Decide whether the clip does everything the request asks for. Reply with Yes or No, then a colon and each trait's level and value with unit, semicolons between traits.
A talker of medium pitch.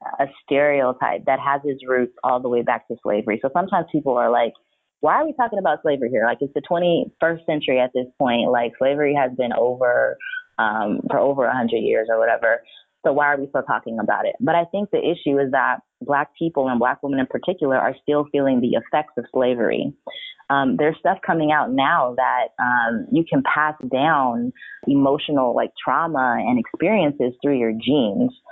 Yes: medium, 145 Hz